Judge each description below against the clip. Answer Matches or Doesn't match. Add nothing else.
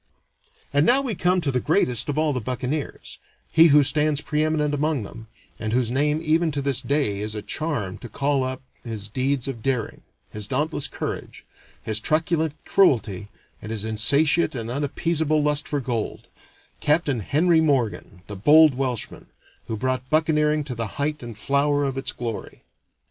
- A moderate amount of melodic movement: Matches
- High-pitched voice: Doesn't match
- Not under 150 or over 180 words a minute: Matches